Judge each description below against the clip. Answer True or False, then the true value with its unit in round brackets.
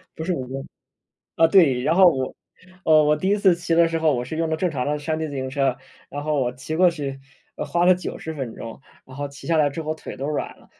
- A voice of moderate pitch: True (155 Hz)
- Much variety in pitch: False (3.3 semitones)